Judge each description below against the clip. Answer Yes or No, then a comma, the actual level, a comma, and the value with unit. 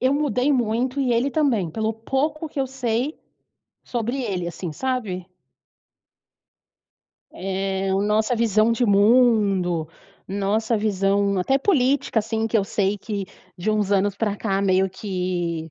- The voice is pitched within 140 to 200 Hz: No, high, 215 Hz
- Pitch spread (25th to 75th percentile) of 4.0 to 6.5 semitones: Yes, average, 4.3 semitones